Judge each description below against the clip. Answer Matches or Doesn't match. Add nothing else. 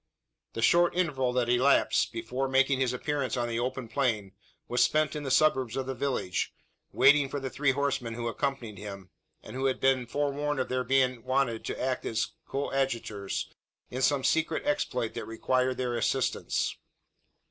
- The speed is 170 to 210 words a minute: Matches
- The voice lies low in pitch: Matches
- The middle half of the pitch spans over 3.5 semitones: Doesn't match